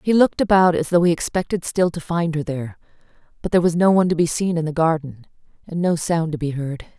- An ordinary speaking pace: No, fast, 250 wpm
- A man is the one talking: No, female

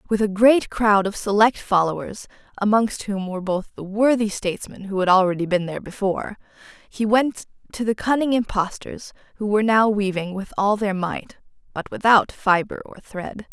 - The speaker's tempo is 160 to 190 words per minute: Yes, average, 175 wpm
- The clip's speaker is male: No, female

